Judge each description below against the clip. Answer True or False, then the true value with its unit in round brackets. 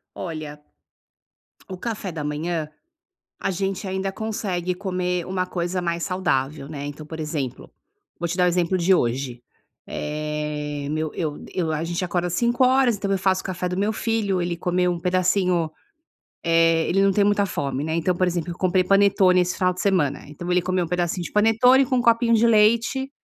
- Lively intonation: False (3.3 semitones)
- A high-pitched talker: False (180 Hz)